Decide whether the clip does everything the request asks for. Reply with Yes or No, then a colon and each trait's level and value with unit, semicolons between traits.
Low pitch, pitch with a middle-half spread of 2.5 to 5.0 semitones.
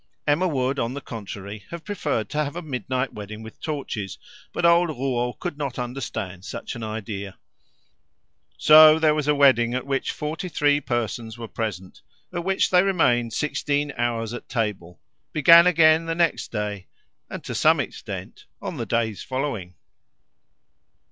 No: low, 130 Hz; wide, 5.6 semitones